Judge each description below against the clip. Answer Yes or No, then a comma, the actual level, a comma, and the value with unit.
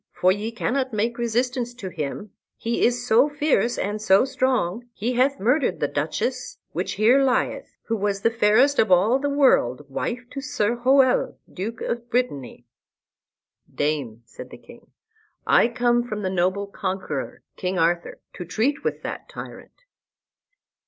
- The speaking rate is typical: Yes, average, 155 wpm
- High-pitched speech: Yes, high, 230 Hz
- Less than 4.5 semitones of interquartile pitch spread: No, average, 4.8 semitones